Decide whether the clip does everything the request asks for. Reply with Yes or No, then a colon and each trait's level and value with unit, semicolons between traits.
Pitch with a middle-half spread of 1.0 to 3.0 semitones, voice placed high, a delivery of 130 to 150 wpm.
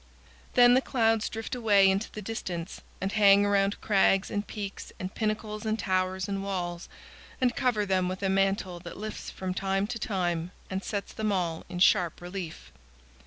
No: narrow, 2.5 semitones; high, 195 Hz; average, 175 wpm